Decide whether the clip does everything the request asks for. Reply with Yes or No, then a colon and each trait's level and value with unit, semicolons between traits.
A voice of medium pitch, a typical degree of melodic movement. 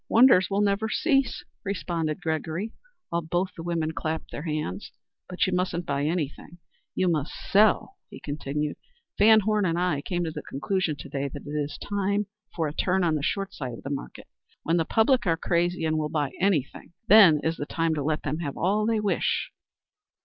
Yes: medium, 170 Hz; average, 4.5 semitones